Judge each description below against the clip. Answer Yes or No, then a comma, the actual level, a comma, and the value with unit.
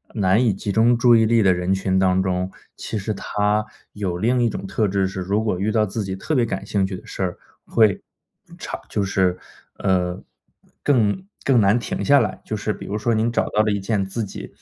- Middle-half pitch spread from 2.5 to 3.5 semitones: Yes, average, 2.9 semitones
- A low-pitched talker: Yes, low, 105 Hz